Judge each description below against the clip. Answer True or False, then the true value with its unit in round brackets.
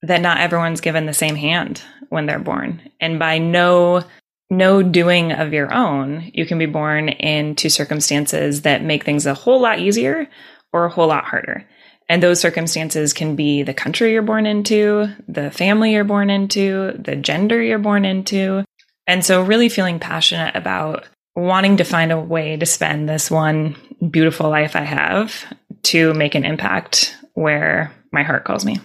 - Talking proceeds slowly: False (175 wpm)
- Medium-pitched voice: True (170 Hz)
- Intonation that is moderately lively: True (4.2 semitones)